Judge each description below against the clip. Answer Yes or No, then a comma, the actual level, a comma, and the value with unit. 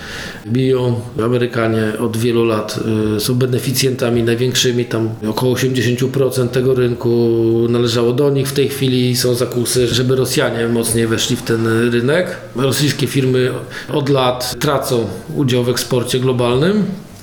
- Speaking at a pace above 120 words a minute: Yes, average, 130 wpm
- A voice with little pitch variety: Yes, narrow, 1.8 semitones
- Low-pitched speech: Yes, low, 125 Hz